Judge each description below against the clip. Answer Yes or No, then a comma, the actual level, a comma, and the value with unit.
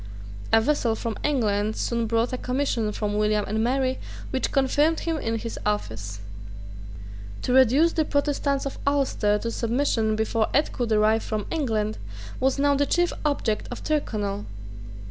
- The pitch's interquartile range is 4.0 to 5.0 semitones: Yes, average, 4.6 semitones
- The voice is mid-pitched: No, high, 235 Hz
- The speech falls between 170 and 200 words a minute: No, average, 155 wpm